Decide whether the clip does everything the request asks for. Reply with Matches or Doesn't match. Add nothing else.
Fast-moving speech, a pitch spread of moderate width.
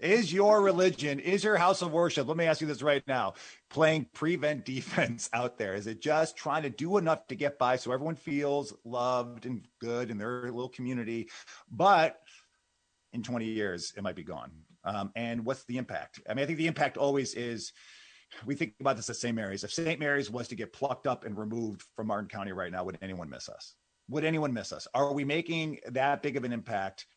Matches